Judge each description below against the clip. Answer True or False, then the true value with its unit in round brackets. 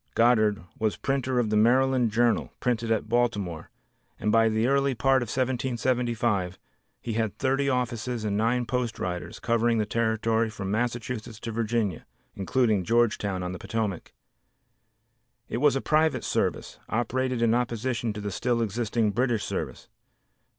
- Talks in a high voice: False (115 Hz)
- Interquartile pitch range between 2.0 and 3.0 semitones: True (2.5 semitones)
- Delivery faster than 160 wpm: False (150 wpm)